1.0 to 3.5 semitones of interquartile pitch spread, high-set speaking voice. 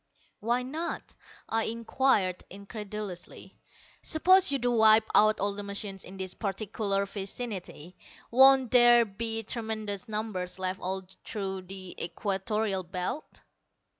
Yes: average, 3.2 semitones; high, 210 Hz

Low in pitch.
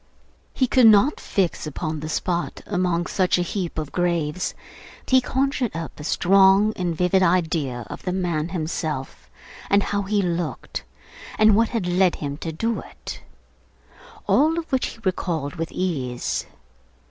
No: medium, 180 Hz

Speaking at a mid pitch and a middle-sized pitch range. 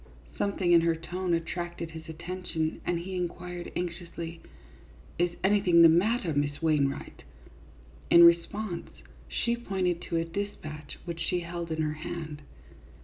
No: medium, 170 Hz; narrow, 1.8 semitones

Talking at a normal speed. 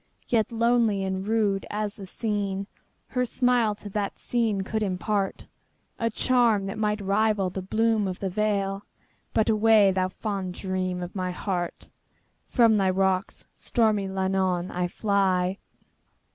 No: slow, 130 wpm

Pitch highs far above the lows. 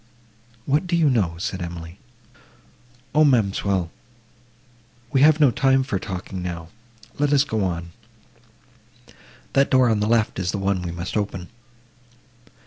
Yes: wide, 6.5 semitones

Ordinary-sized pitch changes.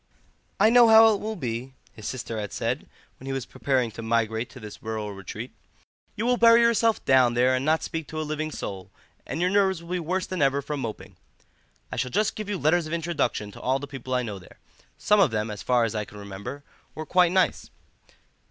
No: wide, 8.0 semitones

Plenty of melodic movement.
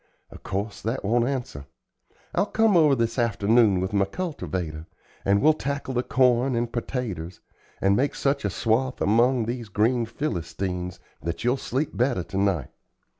No: average, 4.9 semitones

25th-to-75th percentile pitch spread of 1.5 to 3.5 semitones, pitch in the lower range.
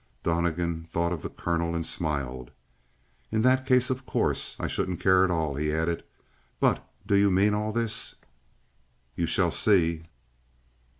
No: average, 4.1 semitones; very low, 85 Hz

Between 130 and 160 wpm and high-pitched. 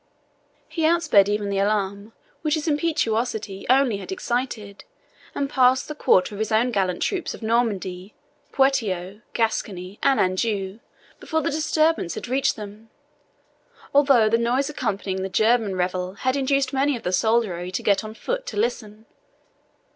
Yes: average, 155 wpm; high, 225 Hz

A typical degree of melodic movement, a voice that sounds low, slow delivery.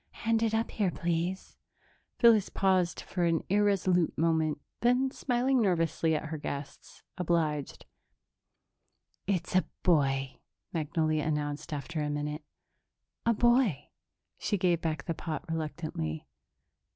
No: average, 4.4 semitones; medium, 165 Hz; slow, 120 wpm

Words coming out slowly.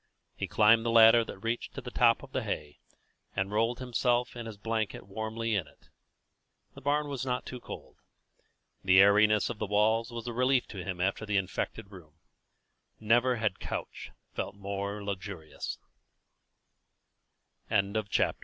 No: average, 150 wpm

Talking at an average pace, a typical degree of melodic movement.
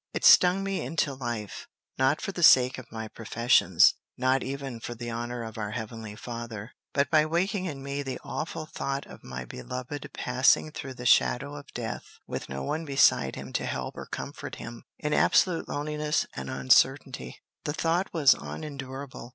Yes: average, 175 wpm; average, 4.5 semitones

